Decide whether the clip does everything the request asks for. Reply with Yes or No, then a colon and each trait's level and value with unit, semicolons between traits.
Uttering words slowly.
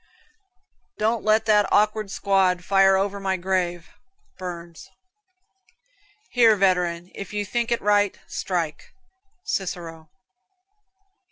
Yes: slow, 100 wpm